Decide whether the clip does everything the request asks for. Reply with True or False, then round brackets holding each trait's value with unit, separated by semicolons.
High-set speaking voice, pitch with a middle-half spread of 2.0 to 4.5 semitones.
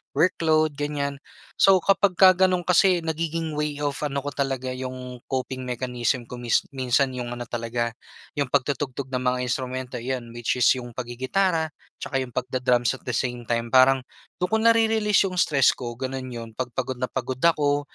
False (130 Hz; 3.4 semitones)